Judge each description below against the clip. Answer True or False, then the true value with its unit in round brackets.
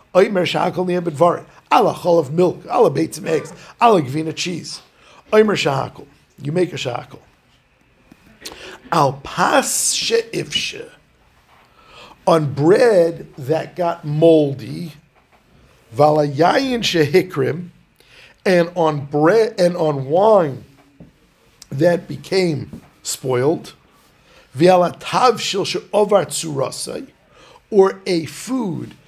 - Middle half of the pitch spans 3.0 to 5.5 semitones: True (3.6 semitones)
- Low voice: False (170 Hz)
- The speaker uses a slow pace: True (100 wpm)